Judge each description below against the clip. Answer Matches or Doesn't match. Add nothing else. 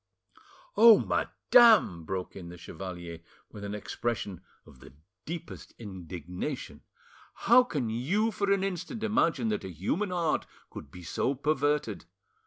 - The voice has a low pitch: Matches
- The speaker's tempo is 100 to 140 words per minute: Matches